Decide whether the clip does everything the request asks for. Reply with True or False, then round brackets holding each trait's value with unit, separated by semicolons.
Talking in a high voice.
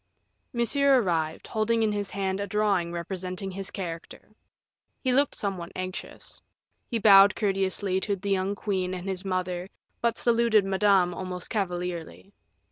True (195 Hz)